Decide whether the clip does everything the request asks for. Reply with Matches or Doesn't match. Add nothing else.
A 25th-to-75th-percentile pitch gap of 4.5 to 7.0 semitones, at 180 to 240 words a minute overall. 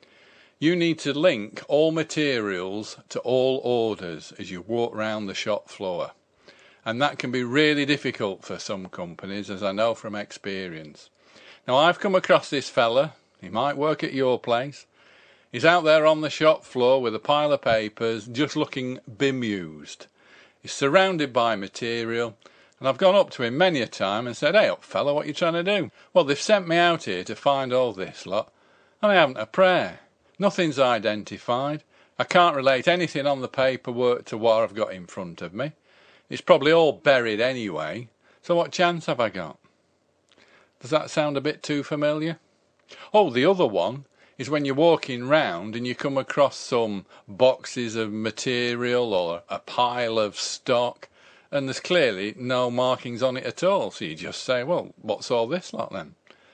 Matches